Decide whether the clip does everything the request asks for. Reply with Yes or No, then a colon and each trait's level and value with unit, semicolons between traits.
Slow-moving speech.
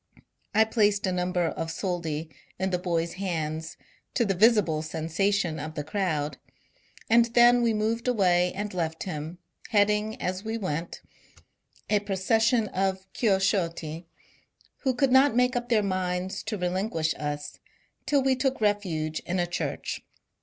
No: average, 145 wpm